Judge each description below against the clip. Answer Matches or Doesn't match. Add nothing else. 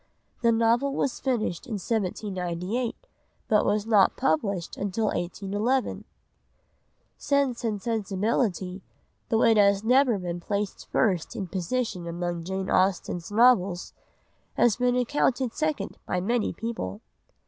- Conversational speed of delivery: Doesn't match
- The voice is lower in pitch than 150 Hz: Doesn't match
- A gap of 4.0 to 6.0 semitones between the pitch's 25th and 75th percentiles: Matches